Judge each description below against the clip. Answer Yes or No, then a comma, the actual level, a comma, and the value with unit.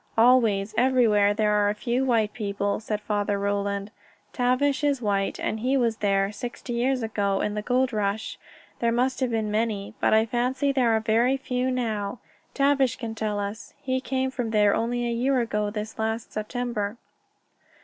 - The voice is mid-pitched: No, high, 225 Hz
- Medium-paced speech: Yes, average, 180 wpm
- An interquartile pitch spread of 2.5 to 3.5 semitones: Yes, average, 3.2 semitones